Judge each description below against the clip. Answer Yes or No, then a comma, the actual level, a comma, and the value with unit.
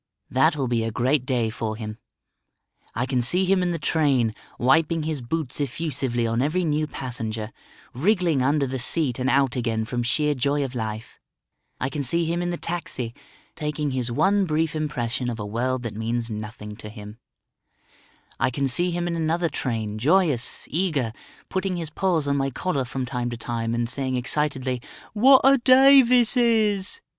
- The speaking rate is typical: Yes, average, 180 wpm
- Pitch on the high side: No, low, 135 Hz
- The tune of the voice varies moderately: No, wide, 5.7 semitones